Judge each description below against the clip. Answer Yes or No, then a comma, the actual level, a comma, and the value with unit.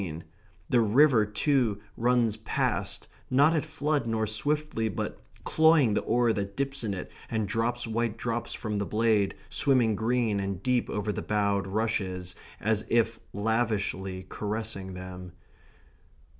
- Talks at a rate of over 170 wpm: No, average, 145 wpm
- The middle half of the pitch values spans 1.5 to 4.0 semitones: Yes, average, 3.1 semitones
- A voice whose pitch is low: Yes, low, 110 Hz